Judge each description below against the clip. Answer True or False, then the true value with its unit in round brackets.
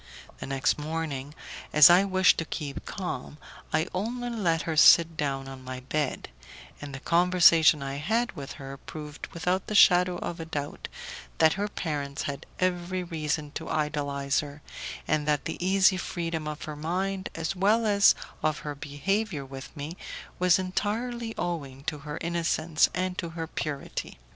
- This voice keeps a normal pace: True (165 wpm)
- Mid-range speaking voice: True (160 Hz)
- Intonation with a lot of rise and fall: False (3.9 semitones)